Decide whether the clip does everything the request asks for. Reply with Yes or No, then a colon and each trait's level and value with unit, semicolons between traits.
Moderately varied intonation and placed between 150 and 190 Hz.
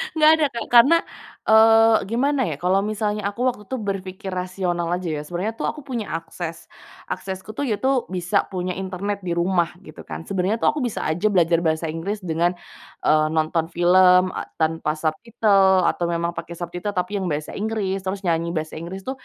Yes: average, 3.7 semitones; medium, 185 Hz